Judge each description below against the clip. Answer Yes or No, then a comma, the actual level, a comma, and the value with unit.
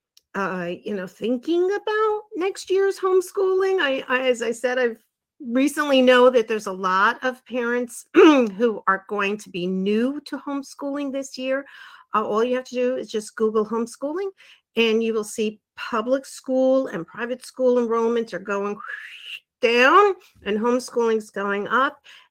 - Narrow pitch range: No, average, 4.5 semitones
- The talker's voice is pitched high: Yes, very high, 250 Hz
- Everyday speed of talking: Yes, average, 160 wpm